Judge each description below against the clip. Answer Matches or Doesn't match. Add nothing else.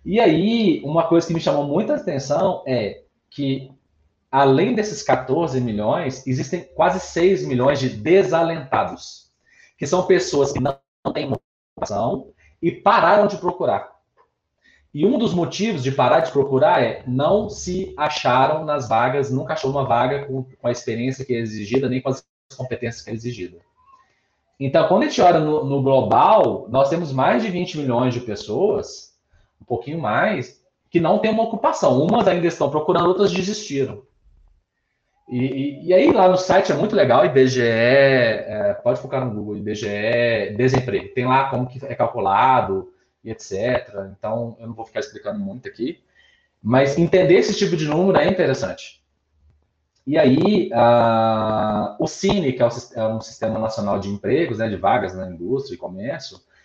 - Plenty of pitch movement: Matches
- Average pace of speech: Matches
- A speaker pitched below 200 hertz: Matches